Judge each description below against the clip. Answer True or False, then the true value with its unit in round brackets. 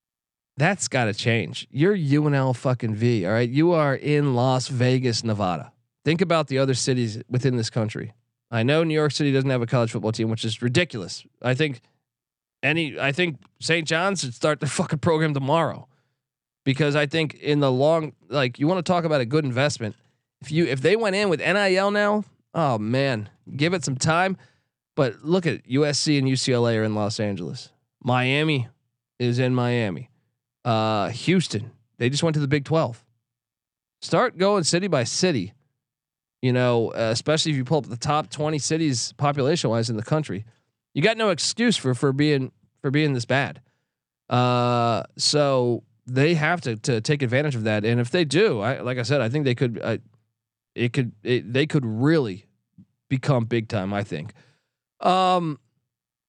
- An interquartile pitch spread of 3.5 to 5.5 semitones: True (4.2 semitones)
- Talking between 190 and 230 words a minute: False (180 wpm)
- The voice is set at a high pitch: False (135 Hz)